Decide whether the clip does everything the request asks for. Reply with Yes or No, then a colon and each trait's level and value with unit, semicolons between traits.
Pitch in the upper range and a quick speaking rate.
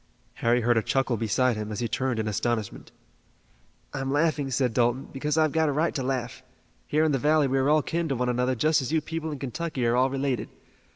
No: low, 135 Hz; fast, 230 wpm